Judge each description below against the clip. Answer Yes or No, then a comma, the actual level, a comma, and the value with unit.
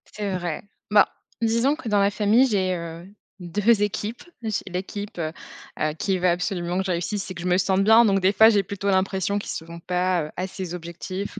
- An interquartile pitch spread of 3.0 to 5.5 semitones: No, narrow, 2.6 semitones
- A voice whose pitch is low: No, high, 190 Hz